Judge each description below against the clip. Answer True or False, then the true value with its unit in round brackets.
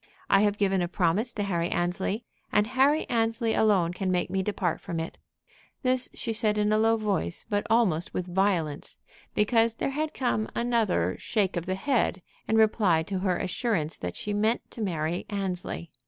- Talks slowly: False (185 wpm)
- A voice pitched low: False (205 Hz)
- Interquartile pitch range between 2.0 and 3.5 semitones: False (4.1 semitones)